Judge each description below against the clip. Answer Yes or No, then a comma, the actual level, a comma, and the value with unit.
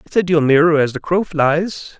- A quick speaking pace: Yes, fast, 240 wpm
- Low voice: No, medium, 160 Hz